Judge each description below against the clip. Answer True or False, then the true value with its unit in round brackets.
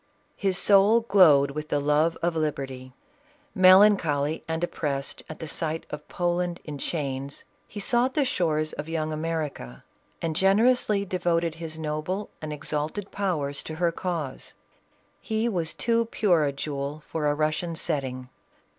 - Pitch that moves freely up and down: False (3.9 semitones)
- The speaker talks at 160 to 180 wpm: False (145 wpm)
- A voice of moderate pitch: True (160 Hz)